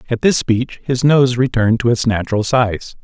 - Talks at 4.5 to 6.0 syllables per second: Yes, 5.1 syllables/s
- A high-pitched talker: No, low, 120 Hz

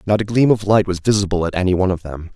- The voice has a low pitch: Yes, very low, 95 Hz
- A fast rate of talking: Yes, fast, 305 wpm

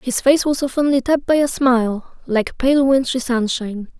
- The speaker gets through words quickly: No, average, 195 wpm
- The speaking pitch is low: No, very high, 255 Hz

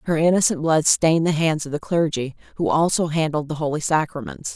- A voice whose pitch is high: No, medium, 155 Hz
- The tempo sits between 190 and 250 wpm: Yes, average, 200 wpm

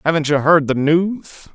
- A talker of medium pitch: Yes, medium, 155 Hz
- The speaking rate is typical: Yes, average, 195 wpm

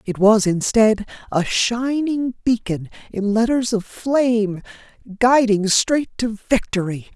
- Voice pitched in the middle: No, high, 220 Hz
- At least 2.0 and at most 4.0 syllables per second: Yes, 3.8 syllables/s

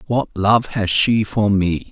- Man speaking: Yes, male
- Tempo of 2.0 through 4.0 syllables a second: Yes, 3.6 syllables/s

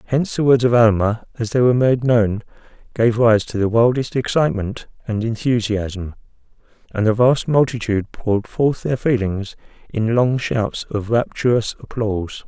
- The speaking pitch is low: Yes, low, 115 Hz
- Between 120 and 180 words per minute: Yes, average, 155 wpm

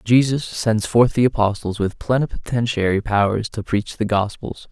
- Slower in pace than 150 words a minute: No, average, 155 wpm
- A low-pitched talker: Yes, low, 110 Hz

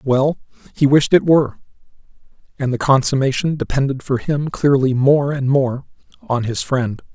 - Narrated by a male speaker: Yes, male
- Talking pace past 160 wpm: No, average, 150 wpm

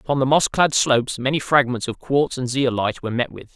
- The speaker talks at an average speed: No, fast, 235 wpm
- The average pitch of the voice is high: No, low, 130 Hz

